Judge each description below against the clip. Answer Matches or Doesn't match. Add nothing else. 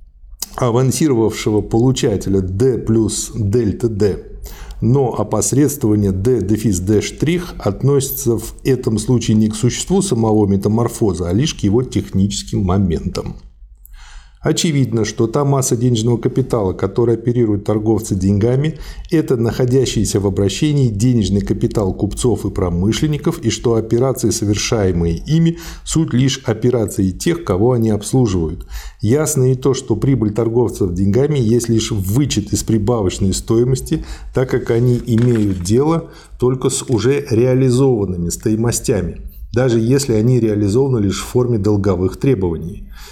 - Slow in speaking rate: Doesn't match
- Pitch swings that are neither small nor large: Matches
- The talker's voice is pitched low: Matches